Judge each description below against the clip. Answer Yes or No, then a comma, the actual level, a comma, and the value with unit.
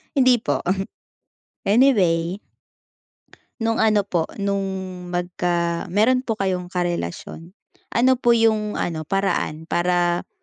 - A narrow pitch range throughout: No, average, 4.2 semitones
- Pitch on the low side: No, high, 190 Hz